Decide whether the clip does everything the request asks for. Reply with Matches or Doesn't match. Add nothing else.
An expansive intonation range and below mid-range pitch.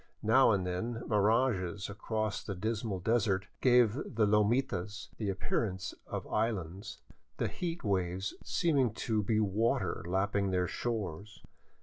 Doesn't match